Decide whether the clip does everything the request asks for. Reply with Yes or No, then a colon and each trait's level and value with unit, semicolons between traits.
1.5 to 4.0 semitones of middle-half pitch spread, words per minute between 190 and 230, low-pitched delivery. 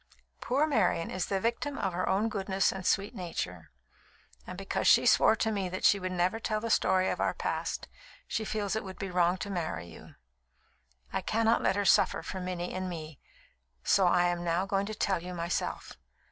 No: average, 3.0 semitones; average, 200 wpm; high, 190 Hz